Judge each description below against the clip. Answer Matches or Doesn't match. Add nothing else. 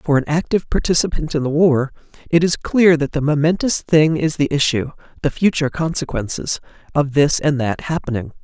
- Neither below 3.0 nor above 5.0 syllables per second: Doesn't match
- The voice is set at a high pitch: Doesn't match